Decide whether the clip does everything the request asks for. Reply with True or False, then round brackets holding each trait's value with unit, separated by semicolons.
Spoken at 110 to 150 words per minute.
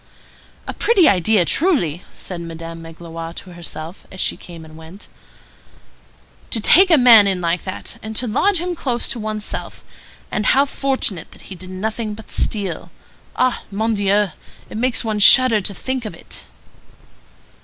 False (165 wpm)